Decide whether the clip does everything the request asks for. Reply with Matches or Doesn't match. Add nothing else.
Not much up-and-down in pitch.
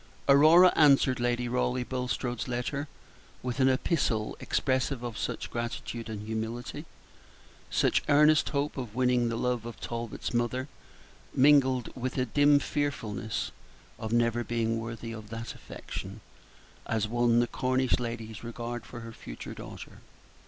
Matches